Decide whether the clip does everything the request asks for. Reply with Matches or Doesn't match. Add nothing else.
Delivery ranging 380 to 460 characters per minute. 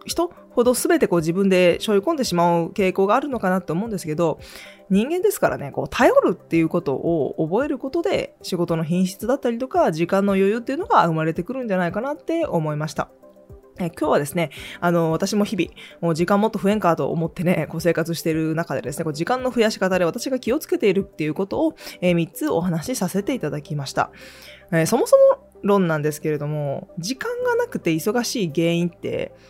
Matches